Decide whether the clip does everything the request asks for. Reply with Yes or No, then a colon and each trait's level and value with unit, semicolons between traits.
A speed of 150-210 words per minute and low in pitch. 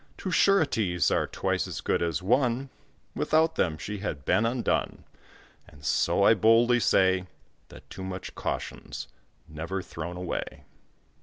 No: average, 140 wpm; low, 100 Hz